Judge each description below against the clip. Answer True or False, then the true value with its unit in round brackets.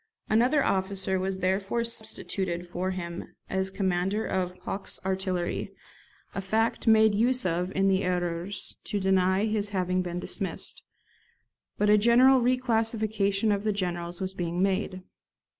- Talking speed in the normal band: True (150 wpm)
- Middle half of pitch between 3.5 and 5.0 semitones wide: False (2.7 semitones)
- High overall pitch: True (195 Hz)